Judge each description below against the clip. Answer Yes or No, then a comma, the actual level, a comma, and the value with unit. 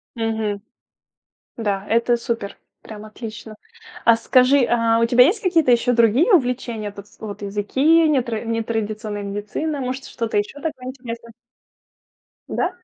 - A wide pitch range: No, average, 3.0 semitones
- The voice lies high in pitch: Yes, high, 230 Hz